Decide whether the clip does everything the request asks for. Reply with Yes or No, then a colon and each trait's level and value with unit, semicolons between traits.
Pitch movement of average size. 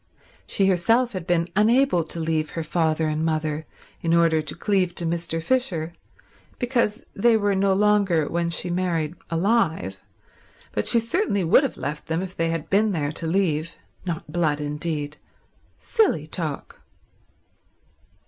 Yes: average, 4.0 semitones